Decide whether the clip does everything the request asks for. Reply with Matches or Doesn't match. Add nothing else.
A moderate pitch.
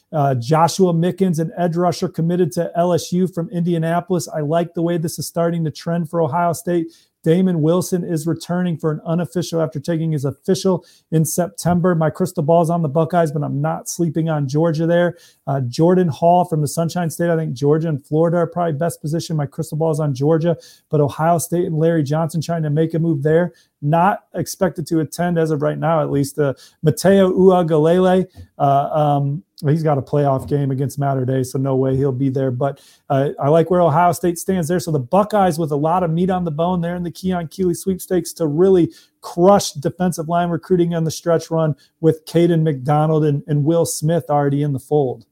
Matches